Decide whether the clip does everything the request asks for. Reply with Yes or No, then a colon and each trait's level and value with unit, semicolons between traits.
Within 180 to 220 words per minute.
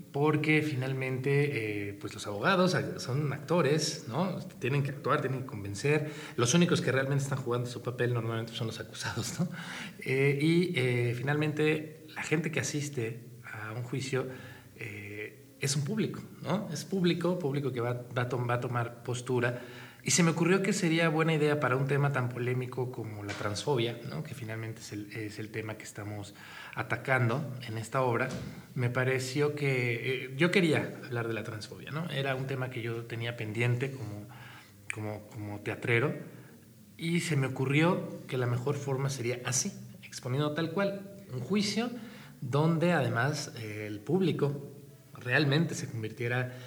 No: average, 165 wpm